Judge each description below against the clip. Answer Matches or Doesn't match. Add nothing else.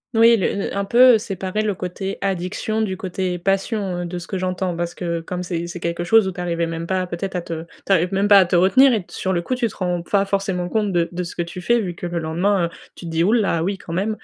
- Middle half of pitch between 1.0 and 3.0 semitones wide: Matches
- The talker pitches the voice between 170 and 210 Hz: Matches